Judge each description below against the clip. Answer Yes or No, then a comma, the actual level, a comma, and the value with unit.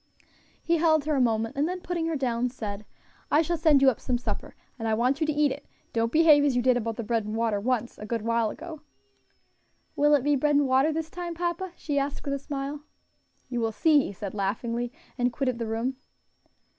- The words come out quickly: Yes, fast, 230 wpm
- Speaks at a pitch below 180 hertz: No, very high, 265 Hz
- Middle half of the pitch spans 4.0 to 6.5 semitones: Yes, average, 4.6 semitones